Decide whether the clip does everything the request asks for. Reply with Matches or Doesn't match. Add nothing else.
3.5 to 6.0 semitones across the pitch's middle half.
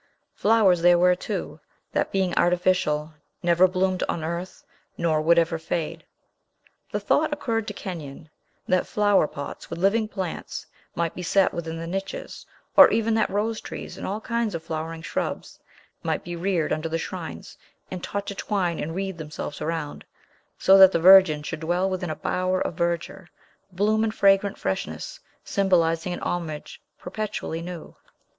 Doesn't match